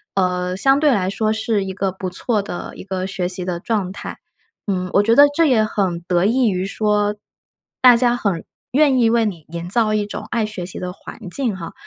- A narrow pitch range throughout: No, average, 3.8 semitones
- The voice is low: No, high, 200 Hz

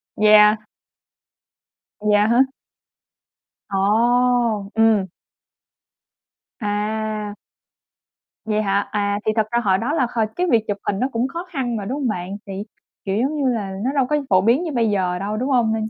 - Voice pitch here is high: Yes, high, 220 Hz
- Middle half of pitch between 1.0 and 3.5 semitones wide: Yes, average, 3.0 semitones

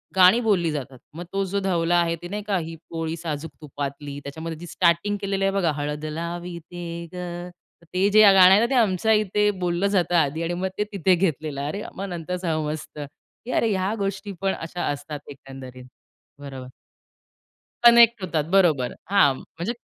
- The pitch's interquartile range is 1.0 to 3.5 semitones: No, average, 4.0 semitones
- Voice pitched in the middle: Yes, medium, 175 Hz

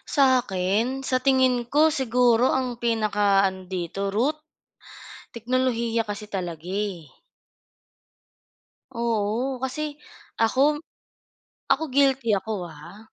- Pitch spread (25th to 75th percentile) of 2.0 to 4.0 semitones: No, average, 4.5 semitones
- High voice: Yes, high, 230 Hz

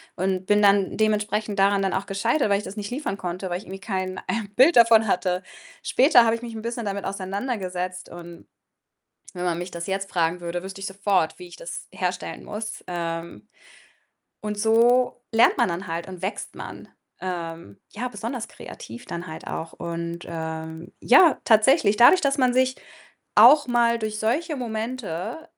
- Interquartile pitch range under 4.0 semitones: No, average, 4.5 semitones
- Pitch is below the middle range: No, high, 200 Hz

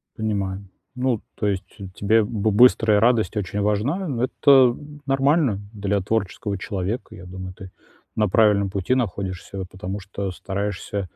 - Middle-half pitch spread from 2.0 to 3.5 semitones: Yes, average, 2.8 semitones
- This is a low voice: Yes, low, 105 Hz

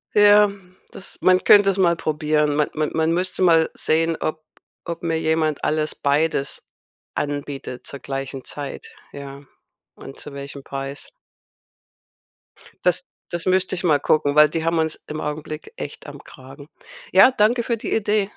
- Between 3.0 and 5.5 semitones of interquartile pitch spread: Yes, average, 3.9 semitones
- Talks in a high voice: No, medium, 155 Hz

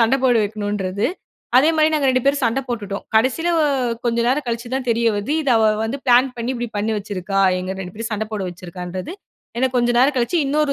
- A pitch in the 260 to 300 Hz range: No, high, 235 Hz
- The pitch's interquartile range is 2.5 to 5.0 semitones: Yes, average, 4.2 semitones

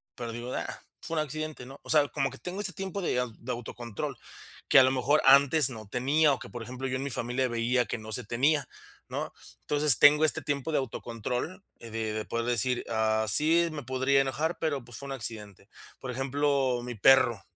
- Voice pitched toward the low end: Yes, low, 130 Hz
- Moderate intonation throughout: Yes, average, 3.6 semitones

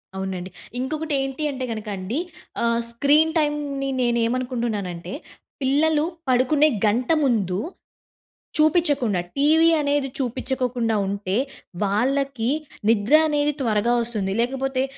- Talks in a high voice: Yes, very high, 255 Hz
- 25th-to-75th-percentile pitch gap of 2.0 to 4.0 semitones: No, average, 4.4 semitones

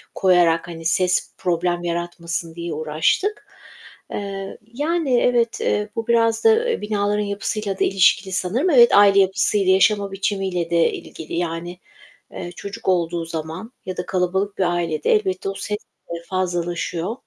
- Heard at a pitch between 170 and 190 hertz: Yes, medium, 185 Hz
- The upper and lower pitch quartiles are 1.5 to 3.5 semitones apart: Yes, average, 3.2 semitones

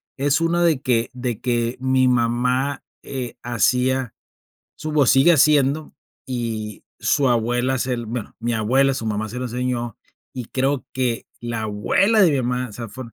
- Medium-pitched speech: No, low, 125 Hz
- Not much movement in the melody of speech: Yes, narrow, 2.2 semitones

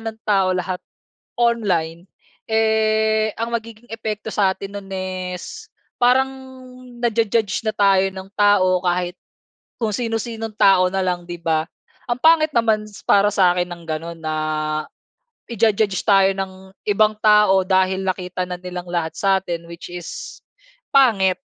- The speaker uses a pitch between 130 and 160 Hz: No, high, 195 Hz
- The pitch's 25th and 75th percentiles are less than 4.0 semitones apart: Yes, average, 3.2 semitones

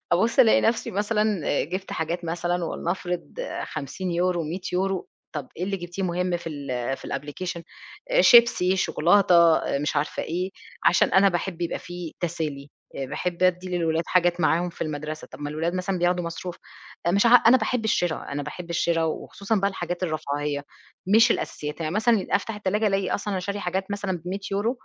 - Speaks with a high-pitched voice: No, medium, 175 Hz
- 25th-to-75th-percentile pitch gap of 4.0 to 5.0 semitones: No, average, 3.1 semitones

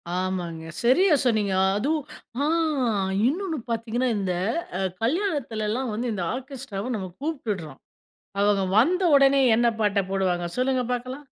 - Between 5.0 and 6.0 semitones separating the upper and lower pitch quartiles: Yes, wide, 5.4 semitones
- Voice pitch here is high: Yes, high, 240 Hz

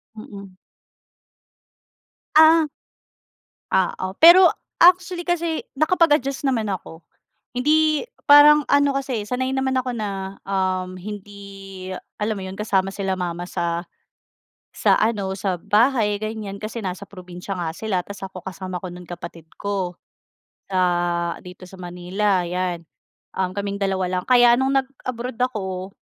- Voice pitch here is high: Yes, high, 200 Hz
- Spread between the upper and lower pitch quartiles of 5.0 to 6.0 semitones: Yes, wide, 5.6 semitones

